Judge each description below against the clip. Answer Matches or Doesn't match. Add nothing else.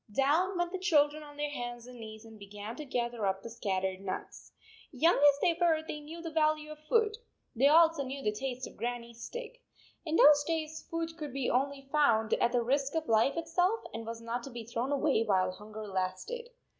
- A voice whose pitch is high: Matches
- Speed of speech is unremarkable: Doesn't match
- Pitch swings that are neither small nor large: Doesn't match